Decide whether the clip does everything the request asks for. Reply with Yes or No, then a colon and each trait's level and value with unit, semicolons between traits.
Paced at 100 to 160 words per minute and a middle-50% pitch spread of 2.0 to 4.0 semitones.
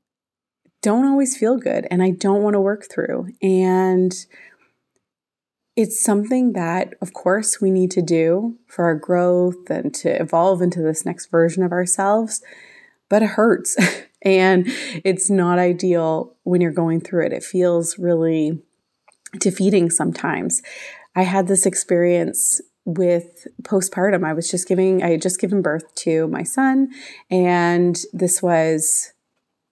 Yes: average, 145 wpm; narrow, 2.5 semitones